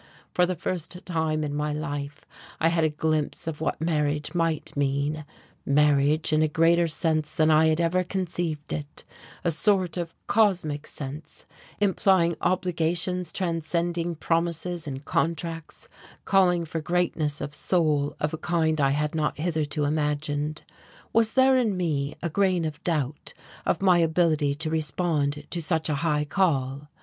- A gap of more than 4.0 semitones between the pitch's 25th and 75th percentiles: No, narrow, 2.6 semitones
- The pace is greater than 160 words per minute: No, average, 155 wpm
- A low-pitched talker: No, medium, 160 Hz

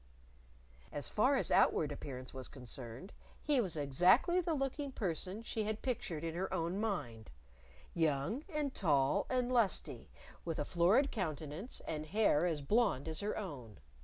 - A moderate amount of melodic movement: No, wide, 7.5 semitones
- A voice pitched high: No, medium, 180 Hz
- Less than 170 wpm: Yes, average, 155 wpm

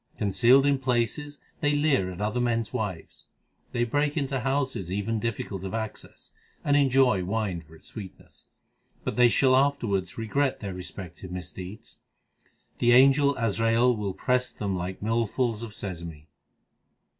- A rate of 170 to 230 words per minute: No, average, 150 wpm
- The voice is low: Yes, low, 115 Hz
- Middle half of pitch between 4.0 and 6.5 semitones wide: Yes, average, 5.3 semitones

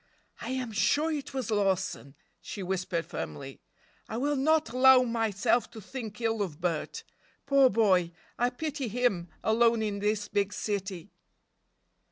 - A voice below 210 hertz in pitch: No, high, 220 Hz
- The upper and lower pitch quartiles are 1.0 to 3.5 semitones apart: No, average, 4.5 semitones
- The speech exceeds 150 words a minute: No, average, 145 wpm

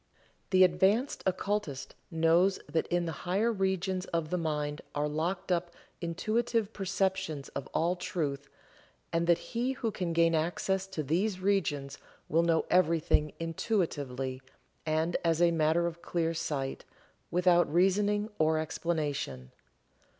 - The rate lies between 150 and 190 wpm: No, slow, 135 wpm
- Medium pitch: Yes, medium, 170 Hz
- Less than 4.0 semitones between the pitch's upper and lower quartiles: Yes, average, 3.3 semitones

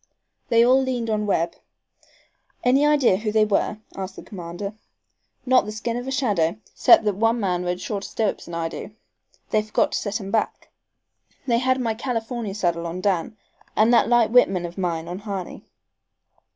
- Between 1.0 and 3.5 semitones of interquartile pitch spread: No, average, 4.3 semitones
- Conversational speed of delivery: Yes, average, 180 wpm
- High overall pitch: Yes, high, 215 Hz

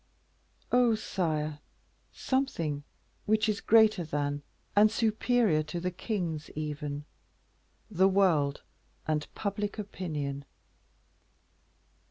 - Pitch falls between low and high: Yes, medium, 180 Hz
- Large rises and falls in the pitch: Yes, wide, 6.1 semitones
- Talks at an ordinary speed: No, slow, 90 wpm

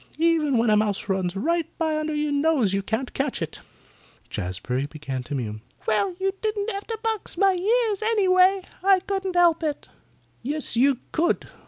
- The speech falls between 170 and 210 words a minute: Yes, average, 175 wpm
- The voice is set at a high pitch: Yes, very high, 310 Hz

